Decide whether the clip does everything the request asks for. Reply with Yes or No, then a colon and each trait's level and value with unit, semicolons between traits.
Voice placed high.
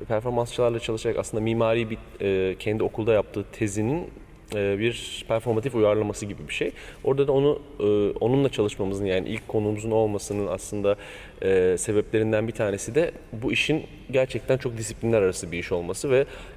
No: low, 110 Hz